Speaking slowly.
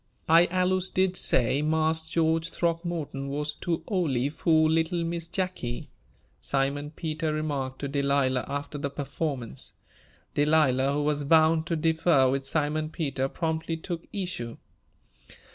Yes: slow, 130 wpm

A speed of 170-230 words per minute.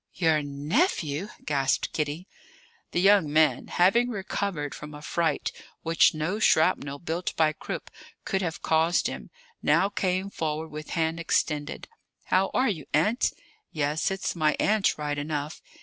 No: average, 145 wpm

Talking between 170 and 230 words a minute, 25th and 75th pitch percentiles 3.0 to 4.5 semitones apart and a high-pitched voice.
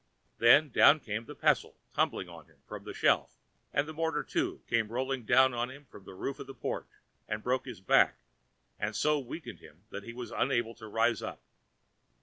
No: average, 200 wpm; average, 3.8 semitones; low, 125 Hz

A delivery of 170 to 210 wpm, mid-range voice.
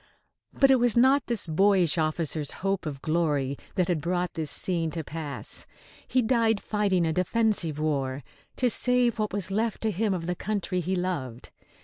Yes: average, 175 wpm; medium, 180 Hz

